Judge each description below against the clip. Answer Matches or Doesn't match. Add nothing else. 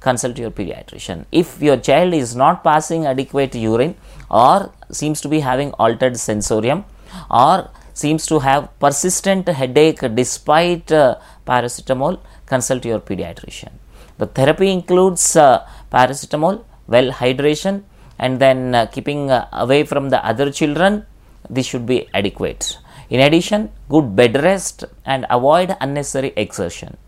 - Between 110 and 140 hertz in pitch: Matches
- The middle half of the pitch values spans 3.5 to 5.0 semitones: Matches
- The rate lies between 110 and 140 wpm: Matches